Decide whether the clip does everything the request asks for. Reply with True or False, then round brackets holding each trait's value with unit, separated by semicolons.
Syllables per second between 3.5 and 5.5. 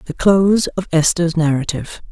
True (5.1 syllables/s)